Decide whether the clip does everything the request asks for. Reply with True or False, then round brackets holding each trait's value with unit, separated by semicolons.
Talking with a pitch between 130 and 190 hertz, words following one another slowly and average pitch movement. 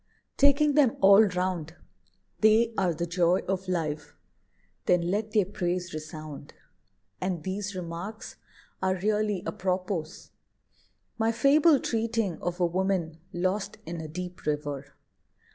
True (185 Hz; 125 wpm; 3.7 semitones)